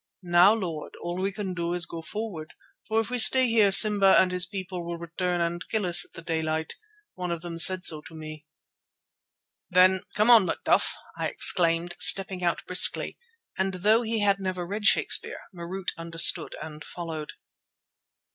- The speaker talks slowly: No, average, 175 wpm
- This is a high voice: No, medium, 180 Hz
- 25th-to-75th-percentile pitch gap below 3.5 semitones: Yes, narrow, 2.6 semitones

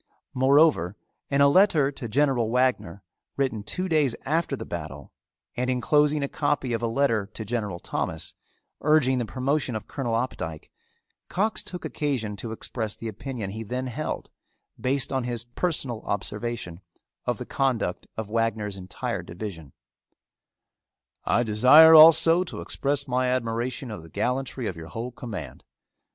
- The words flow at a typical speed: Yes, average, 150 wpm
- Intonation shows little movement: No, average, 4.5 semitones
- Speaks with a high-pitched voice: No, low, 125 Hz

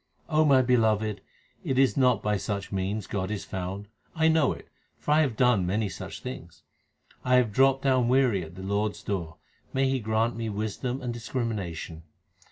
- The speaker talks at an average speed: Yes, average, 180 wpm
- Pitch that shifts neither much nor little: Yes, average, 4.6 semitones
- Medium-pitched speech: No, low, 110 Hz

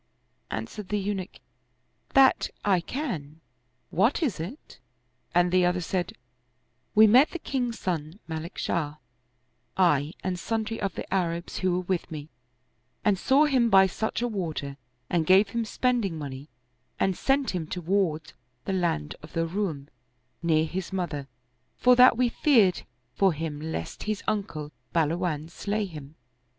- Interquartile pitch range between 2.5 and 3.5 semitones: No, average, 4.9 semitones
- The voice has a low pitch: No, medium, 180 Hz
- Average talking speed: Yes, average, 155 wpm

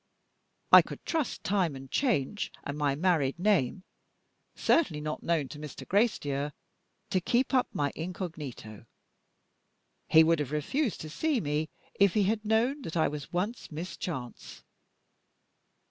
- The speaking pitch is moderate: Yes, medium, 165 Hz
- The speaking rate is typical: Yes, average, 145 wpm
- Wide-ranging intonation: Yes, wide, 6.1 semitones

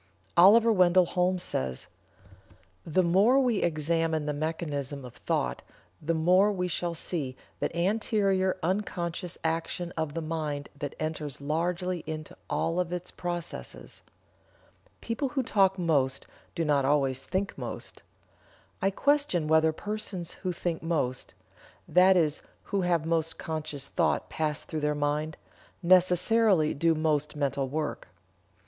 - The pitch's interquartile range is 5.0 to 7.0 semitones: No, average, 3.3 semitones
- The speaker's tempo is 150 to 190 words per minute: No, slow, 135 wpm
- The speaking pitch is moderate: Yes, medium, 165 Hz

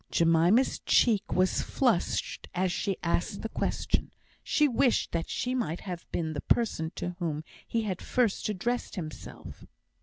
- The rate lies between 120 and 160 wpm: Yes, average, 150 wpm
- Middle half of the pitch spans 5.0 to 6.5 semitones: Yes, wide, 5.5 semitones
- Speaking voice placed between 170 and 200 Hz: Yes, medium, 185 Hz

